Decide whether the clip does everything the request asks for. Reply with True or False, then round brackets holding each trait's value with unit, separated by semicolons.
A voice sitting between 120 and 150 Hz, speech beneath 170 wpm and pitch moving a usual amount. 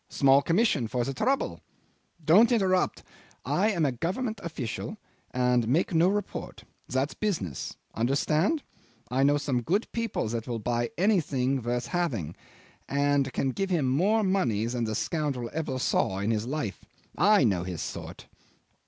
False (140 Hz; 155 wpm; 7.4 semitones)